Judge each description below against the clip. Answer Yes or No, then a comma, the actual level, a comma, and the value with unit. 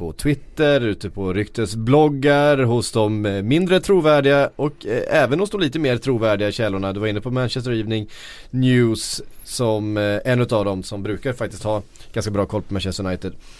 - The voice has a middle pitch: No, low, 110 Hz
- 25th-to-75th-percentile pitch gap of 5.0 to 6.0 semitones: Yes, average, 5.3 semitones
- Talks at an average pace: Yes, average, 175 wpm